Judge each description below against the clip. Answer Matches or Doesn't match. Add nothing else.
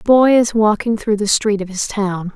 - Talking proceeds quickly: Matches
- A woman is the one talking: Matches